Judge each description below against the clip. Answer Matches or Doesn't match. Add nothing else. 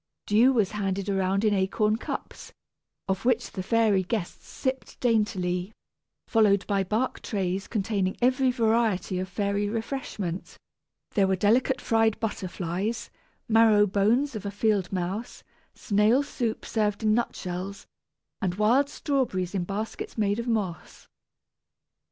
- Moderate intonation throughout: Matches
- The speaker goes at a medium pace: Doesn't match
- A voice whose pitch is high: Matches